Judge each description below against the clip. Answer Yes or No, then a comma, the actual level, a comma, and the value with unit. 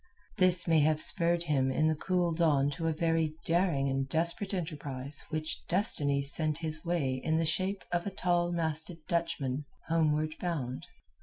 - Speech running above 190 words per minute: No, average, 165 wpm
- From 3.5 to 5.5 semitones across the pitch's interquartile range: No, average, 2.7 semitones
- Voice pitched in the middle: Yes, medium, 160 Hz